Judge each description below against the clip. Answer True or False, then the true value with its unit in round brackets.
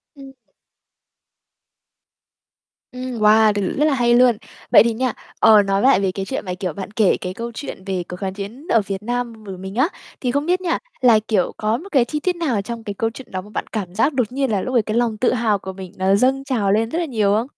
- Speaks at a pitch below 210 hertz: False (225 Hz)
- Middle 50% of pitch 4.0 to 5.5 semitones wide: True (4.3 semitones)